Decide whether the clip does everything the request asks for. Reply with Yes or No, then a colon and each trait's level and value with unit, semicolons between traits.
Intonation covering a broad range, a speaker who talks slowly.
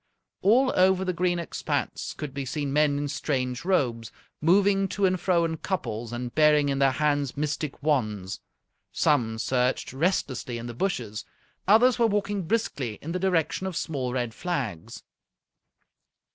No: wide, 6.4 semitones; average, 155 wpm